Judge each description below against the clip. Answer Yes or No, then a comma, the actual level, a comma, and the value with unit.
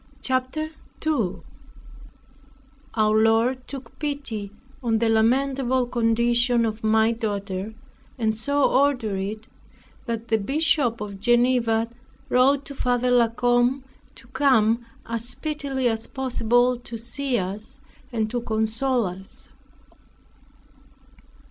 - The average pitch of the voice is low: No, high, 235 Hz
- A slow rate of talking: Yes, slow, 110 wpm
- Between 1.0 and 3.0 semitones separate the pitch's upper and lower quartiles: Yes, average, 2.7 semitones